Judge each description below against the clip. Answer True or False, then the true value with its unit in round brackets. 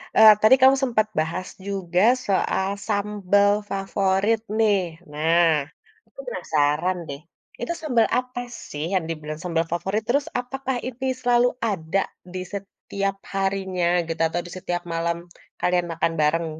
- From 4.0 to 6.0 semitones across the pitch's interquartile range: True (4.3 semitones)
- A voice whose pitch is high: True (195 Hz)